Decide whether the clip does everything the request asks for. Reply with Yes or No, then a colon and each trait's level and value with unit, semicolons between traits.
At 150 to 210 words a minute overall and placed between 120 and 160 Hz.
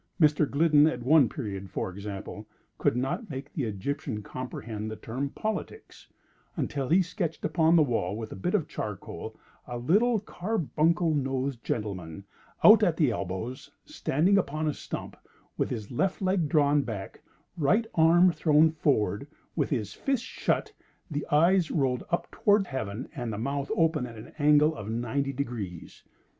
Yes: average, 155 wpm; medium, 140 Hz